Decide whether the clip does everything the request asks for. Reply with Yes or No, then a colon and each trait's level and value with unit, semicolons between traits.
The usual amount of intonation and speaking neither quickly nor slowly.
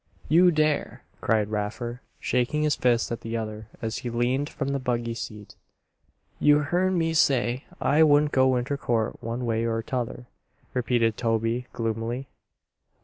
Yes: average, 3.8 semitones; average, 150 wpm